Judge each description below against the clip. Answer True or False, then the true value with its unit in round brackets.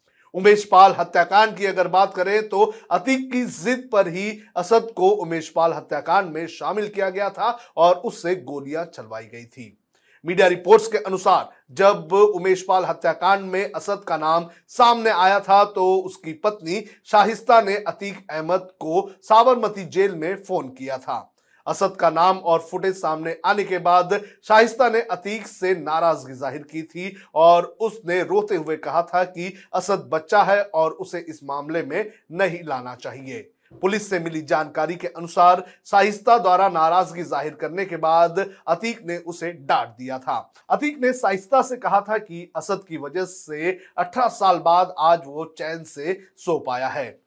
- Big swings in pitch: False (3.7 semitones)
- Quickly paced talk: False (170 wpm)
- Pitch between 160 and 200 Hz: True (185 Hz)